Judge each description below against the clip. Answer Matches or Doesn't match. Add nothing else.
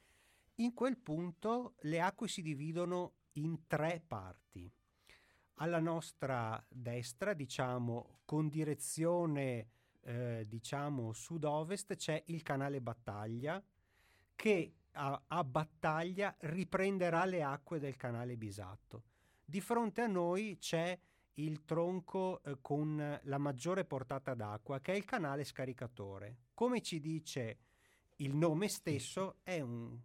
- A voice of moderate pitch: Matches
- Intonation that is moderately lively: Doesn't match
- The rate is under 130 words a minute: Matches